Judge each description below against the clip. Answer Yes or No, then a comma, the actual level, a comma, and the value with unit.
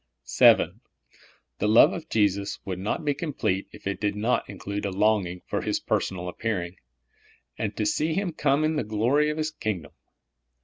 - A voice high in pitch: No, low, 105 Hz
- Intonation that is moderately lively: No, wide, 7.1 semitones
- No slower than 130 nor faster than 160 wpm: No, average, 175 wpm